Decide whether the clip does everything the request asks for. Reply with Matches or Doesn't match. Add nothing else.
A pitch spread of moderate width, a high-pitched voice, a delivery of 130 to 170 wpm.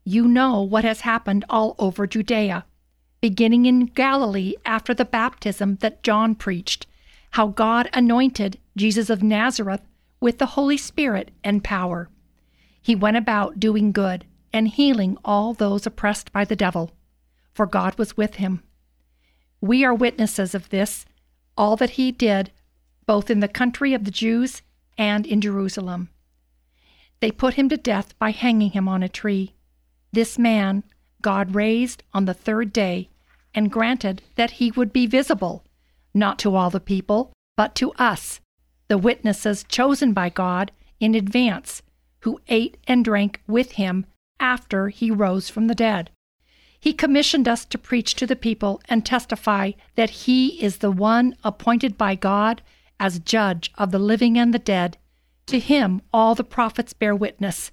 Matches